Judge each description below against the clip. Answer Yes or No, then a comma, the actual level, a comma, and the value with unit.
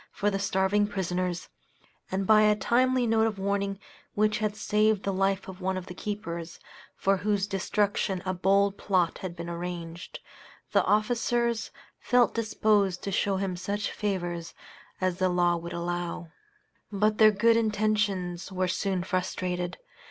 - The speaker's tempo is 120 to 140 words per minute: No, average, 150 wpm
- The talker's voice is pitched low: No, high, 195 Hz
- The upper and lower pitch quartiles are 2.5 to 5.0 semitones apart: Yes, average, 2.8 semitones